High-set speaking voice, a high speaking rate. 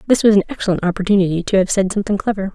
Yes: high, 195 Hz; fast, 235 wpm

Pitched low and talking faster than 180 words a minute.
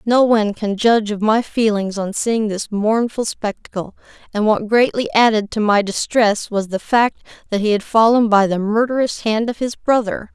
No: high, 215 Hz; average, 190 wpm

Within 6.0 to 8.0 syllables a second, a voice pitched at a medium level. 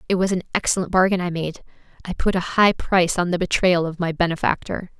Yes: 6.3 syllables/s; medium, 180 Hz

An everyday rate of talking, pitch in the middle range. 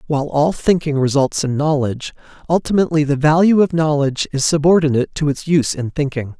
Yes: average, 170 wpm; medium, 150 Hz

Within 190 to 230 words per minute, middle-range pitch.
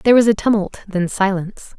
No: average, 200 wpm; high, 205 Hz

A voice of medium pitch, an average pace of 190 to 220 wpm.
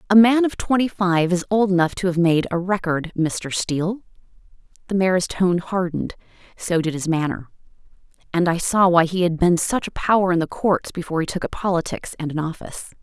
Yes: medium, 180 Hz; fast, 205 wpm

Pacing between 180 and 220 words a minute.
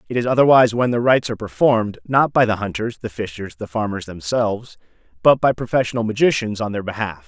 Yes: average, 200 wpm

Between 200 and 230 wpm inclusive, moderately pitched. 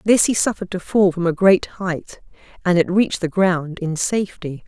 Yes: fast, 205 wpm; medium, 180 Hz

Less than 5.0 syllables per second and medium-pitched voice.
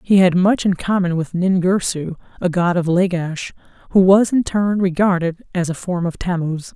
Yes: 4.7 syllables/s; medium, 180 Hz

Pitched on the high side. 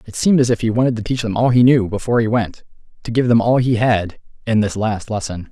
No: low, 115 Hz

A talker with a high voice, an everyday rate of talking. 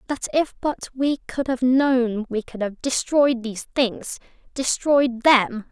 No: very high, 250 Hz; slow, 125 wpm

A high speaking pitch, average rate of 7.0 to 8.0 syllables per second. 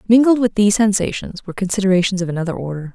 Yes: high, 200 Hz; 7.5 syllables/s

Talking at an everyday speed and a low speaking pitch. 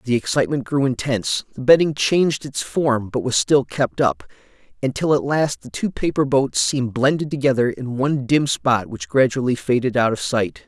Yes: average, 190 wpm; low, 130 Hz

